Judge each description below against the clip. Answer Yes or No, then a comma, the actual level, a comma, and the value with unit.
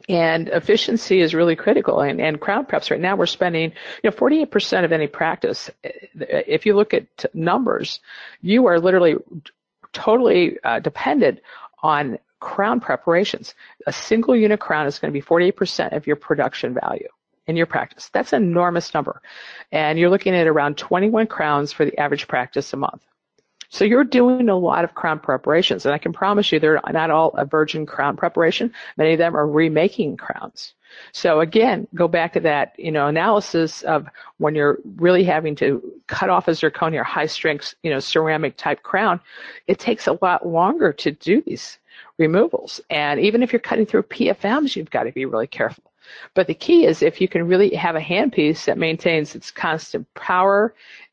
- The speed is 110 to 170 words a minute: No, average, 185 wpm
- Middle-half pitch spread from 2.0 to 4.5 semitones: No, average, 4.9 semitones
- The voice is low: No, medium, 170 Hz